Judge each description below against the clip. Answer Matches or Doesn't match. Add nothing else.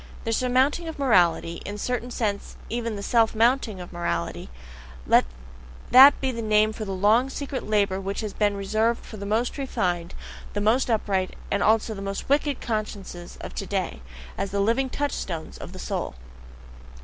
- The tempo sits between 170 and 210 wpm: Matches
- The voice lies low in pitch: Doesn't match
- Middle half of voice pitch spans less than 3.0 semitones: Doesn't match